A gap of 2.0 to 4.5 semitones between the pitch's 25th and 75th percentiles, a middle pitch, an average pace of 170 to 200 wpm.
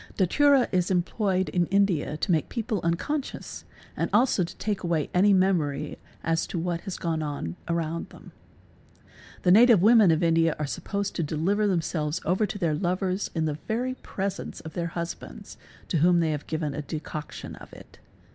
Yes: average, 3.8 semitones; medium, 175 Hz; average, 185 wpm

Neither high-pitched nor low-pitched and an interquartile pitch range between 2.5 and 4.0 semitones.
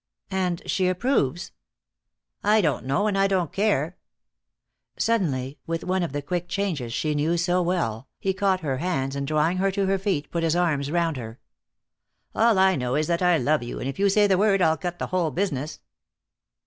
No: medium, 175 Hz; average, 4.7 semitones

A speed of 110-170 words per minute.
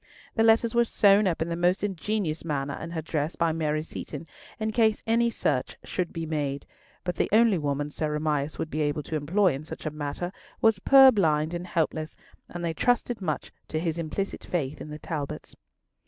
No: average, 200 wpm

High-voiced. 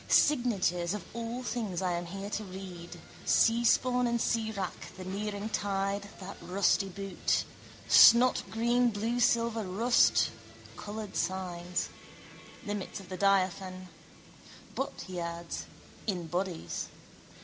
Yes: high, 200 Hz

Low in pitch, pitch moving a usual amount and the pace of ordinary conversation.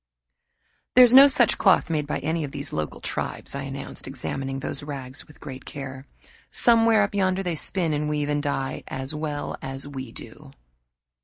No: medium, 145 Hz; average, 3.9 semitones; average, 180 wpm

